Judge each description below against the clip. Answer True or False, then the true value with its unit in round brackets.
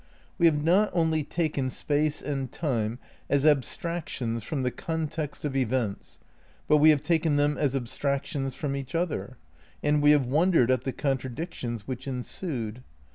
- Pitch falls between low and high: True (145 Hz)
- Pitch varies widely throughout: False (3.3 semitones)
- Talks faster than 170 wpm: False (160 wpm)